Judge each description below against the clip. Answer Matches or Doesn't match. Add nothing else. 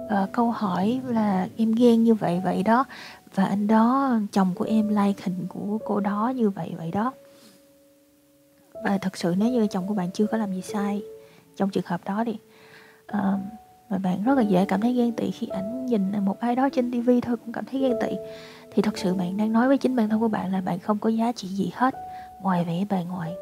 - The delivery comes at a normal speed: Matches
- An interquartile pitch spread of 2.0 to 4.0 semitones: Matches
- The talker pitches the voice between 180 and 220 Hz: Matches